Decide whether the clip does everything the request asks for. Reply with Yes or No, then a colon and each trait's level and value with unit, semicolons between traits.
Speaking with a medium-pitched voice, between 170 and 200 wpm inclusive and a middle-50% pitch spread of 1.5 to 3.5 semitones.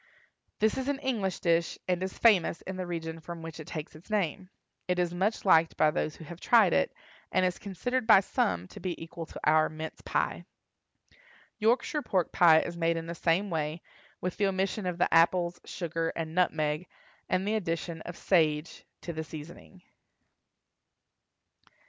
Yes: medium, 175 Hz; average, 180 wpm; average, 2.7 semitones